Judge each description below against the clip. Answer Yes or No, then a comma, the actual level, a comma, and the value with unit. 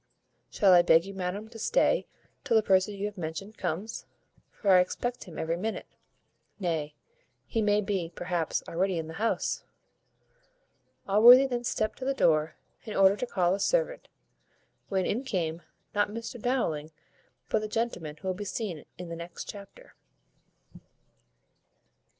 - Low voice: No, high, 195 Hz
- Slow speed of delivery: No, average, 155 wpm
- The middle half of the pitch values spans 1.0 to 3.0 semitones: No, average, 4.3 semitones